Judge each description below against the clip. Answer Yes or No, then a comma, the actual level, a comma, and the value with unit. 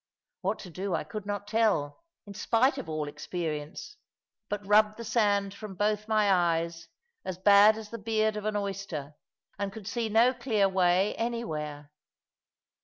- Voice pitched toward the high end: Yes, high, 205 Hz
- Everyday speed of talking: Yes, average, 165 wpm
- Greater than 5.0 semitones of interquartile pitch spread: No, average, 3.5 semitones